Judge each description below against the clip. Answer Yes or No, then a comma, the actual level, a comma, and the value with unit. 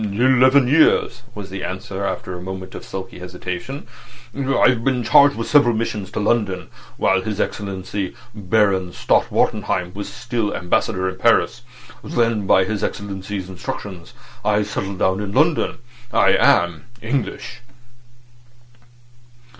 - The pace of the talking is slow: Yes, slow, 130 wpm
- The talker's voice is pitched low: Yes, low, 100 Hz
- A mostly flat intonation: No, average, 3.8 semitones